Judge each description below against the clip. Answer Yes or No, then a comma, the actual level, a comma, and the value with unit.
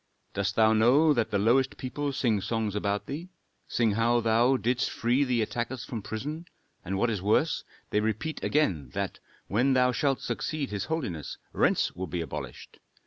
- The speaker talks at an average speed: Yes, average, 175 wpm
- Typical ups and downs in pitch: Yes, average, 4.2 semitones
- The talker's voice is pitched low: Yes, low, 115 Hz